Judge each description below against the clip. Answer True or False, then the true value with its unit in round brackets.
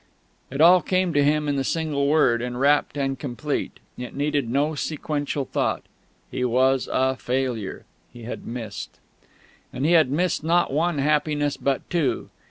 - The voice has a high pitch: False (140 Hz)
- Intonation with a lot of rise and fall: False (2.8 semitones)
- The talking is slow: False (160 wpm)